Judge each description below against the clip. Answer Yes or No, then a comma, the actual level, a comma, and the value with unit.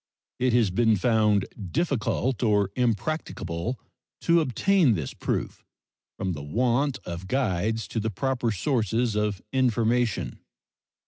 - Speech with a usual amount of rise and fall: Yes, average, 4.0 semitones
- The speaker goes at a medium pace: No, slow, 120 wpm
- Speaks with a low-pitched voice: Yes, low, 115 Hz